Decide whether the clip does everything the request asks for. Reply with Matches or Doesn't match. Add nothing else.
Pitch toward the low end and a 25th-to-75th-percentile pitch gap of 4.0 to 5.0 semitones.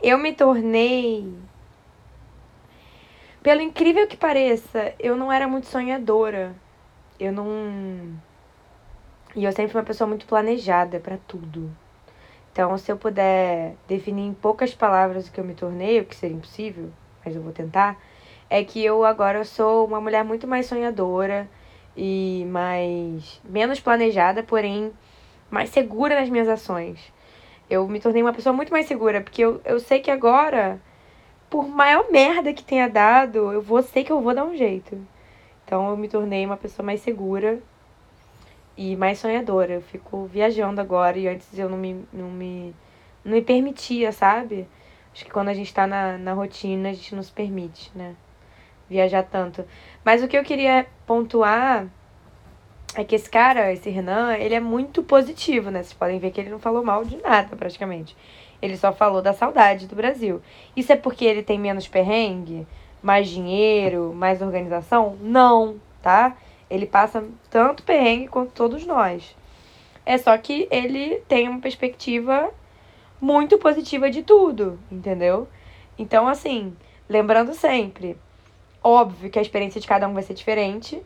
Doesn't match